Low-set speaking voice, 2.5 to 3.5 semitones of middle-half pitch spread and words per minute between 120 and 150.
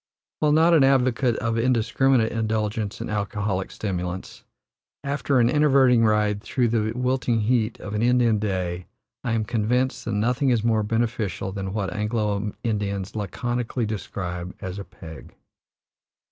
Yes: low, 110 Hz; average, 3.2 semitones; average, 145 wpm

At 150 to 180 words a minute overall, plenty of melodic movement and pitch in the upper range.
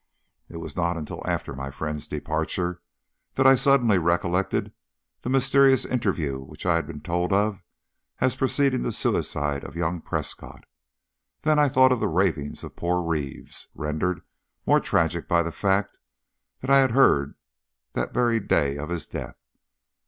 No: average, 160 wpm; wide, 7.9 semitones; very low, 90 Hz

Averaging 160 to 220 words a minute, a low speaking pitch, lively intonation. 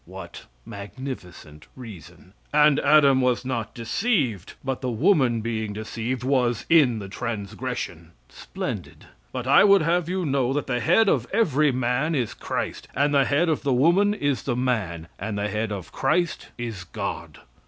No: average, 165 wpm; low, 125 Hz; average, 5.0 semitones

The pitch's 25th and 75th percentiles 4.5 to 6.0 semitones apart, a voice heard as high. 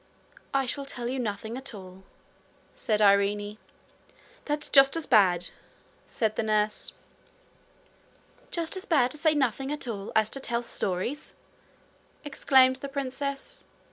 Yes: average, 4.8 semitones; very high, 250 Hz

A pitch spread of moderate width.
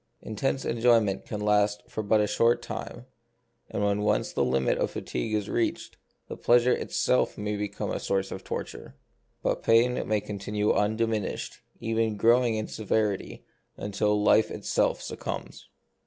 No: narrow, 1.7 semitones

